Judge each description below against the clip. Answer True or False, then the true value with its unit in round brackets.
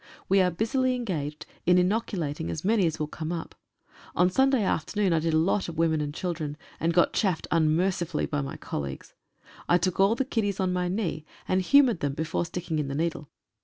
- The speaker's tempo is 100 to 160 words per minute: False (200 wpm)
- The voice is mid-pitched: True (175 Hz)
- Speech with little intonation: False (3.7 semitones)